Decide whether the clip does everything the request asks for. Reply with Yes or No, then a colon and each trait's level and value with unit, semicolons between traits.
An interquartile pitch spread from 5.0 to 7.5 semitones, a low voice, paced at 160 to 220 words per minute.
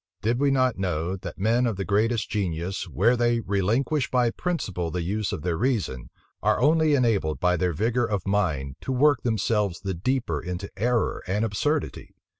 Yes: average, 5.3 semitones; low, 105 Hz; average, 180 wpm